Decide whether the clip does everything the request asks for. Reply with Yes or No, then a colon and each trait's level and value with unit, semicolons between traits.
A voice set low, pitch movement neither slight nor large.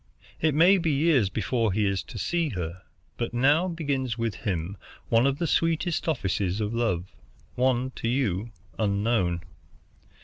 No: low, 120 Hz; wide, 6.7 semitones